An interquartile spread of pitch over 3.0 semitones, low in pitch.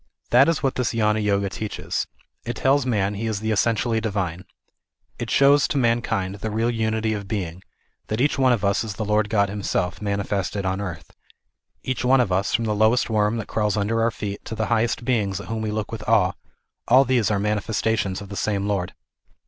No: narrow, 2.4 semitones; low, 110 Hz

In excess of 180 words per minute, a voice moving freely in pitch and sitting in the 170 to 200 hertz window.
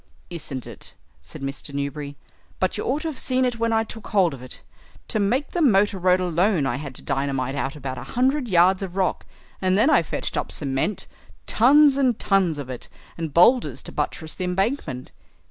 Yes: average, 200 wpm; wide, 8.3 semitones; medium, 185 Hz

